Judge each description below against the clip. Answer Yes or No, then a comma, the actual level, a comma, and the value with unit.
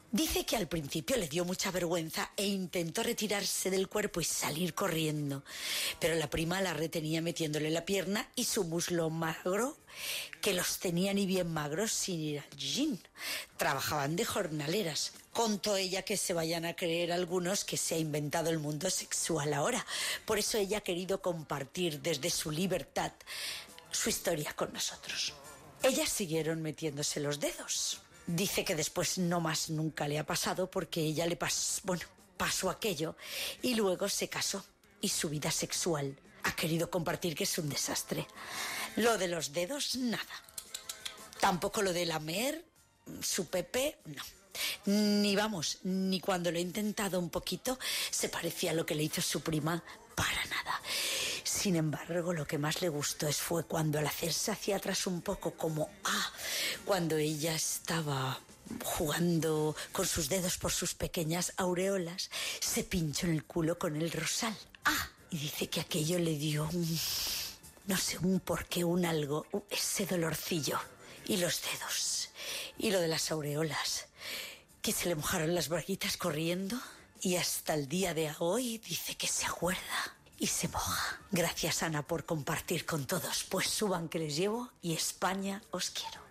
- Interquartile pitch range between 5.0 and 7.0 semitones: No, average, 3.4 semitones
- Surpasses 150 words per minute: Yes, average, 165 wpm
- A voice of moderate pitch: Yes, medium, 175 Hz